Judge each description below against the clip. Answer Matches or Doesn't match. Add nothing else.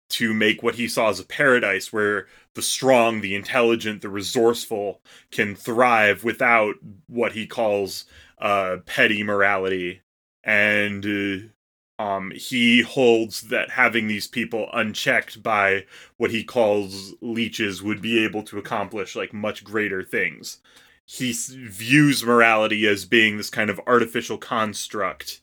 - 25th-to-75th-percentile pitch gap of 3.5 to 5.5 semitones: Doesn't match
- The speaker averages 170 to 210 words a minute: Doesn't match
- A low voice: Matches